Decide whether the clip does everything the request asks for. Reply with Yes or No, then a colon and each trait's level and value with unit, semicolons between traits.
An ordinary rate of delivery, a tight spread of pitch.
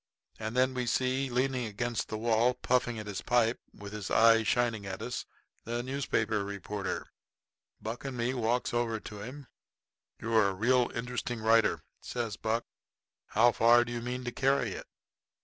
Yes: average, 165 wpm; narrow, 2.1 semitones